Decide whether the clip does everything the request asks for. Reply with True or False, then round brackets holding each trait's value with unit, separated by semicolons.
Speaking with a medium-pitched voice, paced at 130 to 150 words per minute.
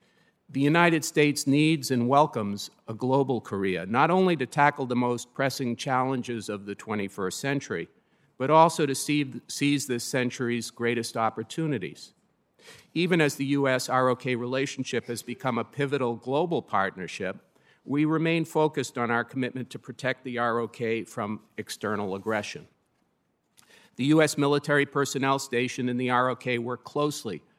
False (130 Hz; 140 wpm)